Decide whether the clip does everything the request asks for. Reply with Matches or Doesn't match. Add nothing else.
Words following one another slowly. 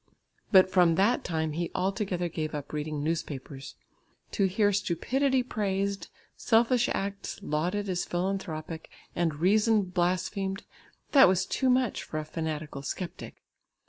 Matches